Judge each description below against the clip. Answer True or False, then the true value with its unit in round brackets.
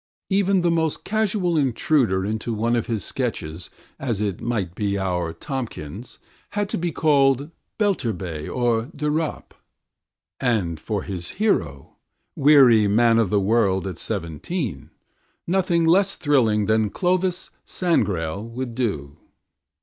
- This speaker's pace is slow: True (130 wpm)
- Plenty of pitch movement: True (8.2 semitones)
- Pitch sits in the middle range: False (115 Hz)